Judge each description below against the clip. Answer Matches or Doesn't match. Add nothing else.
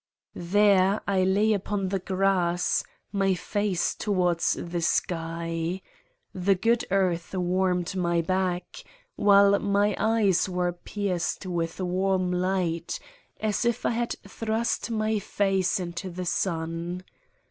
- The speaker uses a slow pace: Matches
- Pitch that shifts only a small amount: Matches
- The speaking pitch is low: Doesn't match